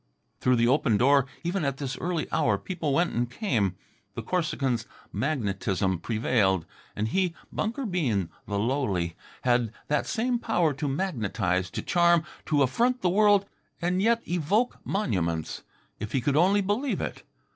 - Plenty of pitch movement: Yes, wide, 8.7 semitones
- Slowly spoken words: No, average, 155 wpm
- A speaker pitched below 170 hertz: Yes, medium, 140 Hz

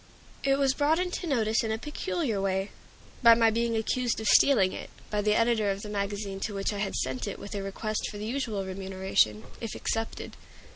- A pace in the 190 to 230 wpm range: Yes, fast, 205 wpm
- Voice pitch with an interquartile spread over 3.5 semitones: No, average, 3.1 semitones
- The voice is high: Yes, high, 215 Hz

